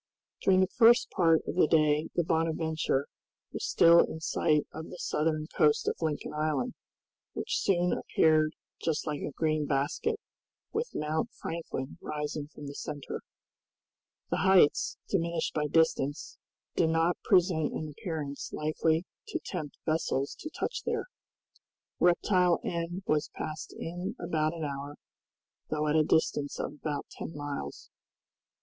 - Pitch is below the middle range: No, medium, 160 Hz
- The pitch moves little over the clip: Yes, narrow, 2.3 semitones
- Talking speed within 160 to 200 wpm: No, average, 145 wpm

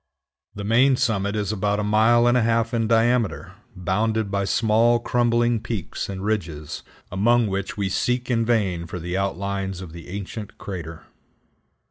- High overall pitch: No, low, 105 Hz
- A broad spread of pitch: No, average, 3.3 semitones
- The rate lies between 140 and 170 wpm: Yes, average, 160 wpm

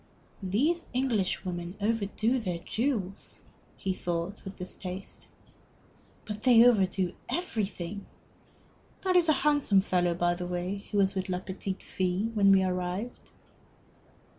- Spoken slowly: Yes, slow, 125 wpm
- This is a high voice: Yes, high, 195 Hz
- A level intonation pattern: No, average, 3.8 semitones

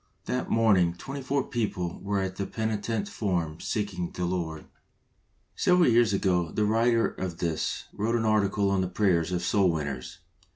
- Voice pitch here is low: Yes, low, 100 Hz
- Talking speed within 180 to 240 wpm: No, average, 165 wpm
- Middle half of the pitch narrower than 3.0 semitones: No, average, 4.2 semitones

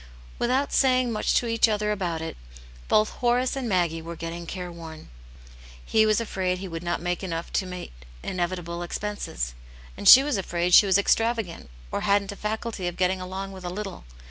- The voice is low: No, high, 190 Hz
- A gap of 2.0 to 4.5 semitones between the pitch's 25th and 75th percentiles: Yes, average, 3.7 semitones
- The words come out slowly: No, average, 180 wpm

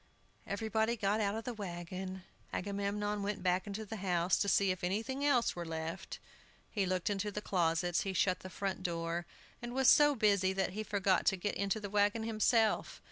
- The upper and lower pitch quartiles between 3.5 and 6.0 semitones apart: No, average, 2.7 semitones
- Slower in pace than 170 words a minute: No, average, 190 wpm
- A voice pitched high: Yes, high, 200 Hz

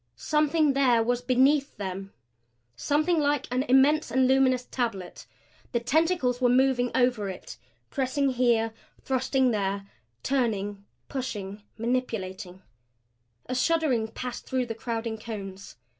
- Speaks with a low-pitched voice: No, very high, 250 Hz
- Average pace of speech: No, slow, 120 wpm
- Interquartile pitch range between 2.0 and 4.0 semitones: Yes, average, 3.4 semitones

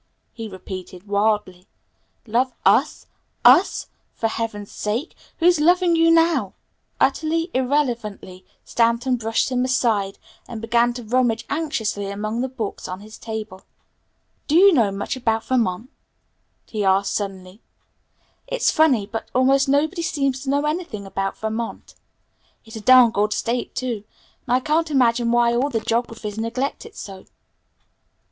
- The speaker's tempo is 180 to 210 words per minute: No, average, 140 wpm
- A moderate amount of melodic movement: Yes, average, 4.2 semitones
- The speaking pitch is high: Yes, high, 235 Hz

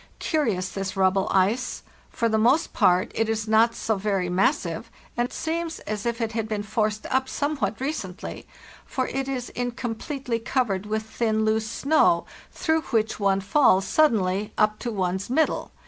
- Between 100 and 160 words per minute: No, average, 170 wpm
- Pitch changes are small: No, average, 4.2 semitones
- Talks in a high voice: Yes, high, 220 Hz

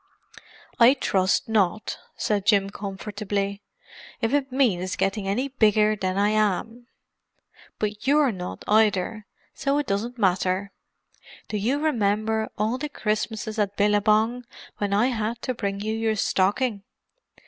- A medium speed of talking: No, slow, 130 wpm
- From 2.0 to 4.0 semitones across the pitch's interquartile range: Yes, average, 2.8 semitones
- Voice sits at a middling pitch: No, high, 215 Hz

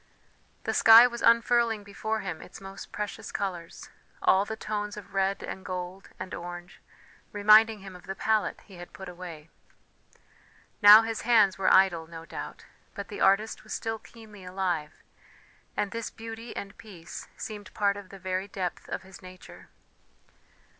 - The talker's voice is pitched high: Yes, high, 200 Hz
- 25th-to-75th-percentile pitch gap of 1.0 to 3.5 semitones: Yes, average, 2.8 semitones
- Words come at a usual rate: Yes, average, 160 wpm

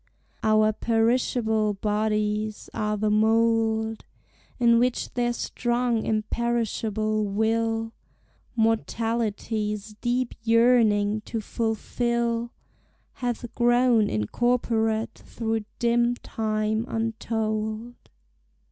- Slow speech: Yes, slow, 75 wpm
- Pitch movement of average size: No, narrow, 1.7 semitones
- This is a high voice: Yes, high, 225 Hz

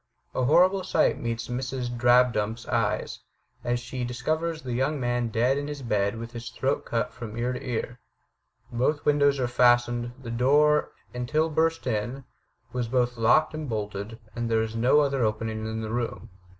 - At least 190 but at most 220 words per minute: No, average, 175 wpm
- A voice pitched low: Yes, low, 120 Hz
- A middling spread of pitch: Yes, average, 3.0 semitones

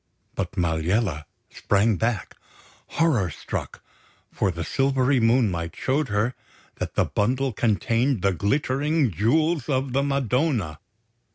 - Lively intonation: Yes, wide, 5.8 semitones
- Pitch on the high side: No, low, 120 Hz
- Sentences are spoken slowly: Yes, slow, 115 wpm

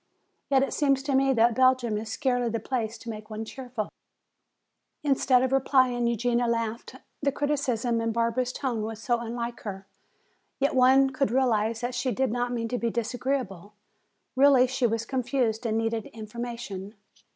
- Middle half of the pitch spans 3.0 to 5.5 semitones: No, narrow, 2.5 semitones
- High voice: Yes, high, 240 Hz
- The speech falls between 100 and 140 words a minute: No, average, 165 wpm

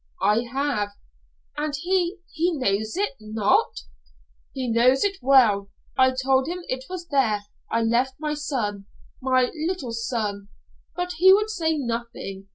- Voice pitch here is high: Yes, very high, 260 Hz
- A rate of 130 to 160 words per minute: Yes, average, 145 wpm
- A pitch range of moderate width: No, wide, 5.9 semitones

